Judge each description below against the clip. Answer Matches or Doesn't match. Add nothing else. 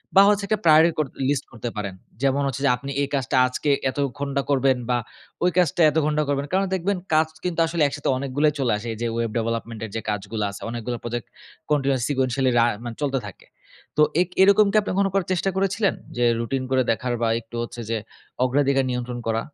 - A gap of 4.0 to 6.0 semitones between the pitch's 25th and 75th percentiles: Matches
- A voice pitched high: Doesn't match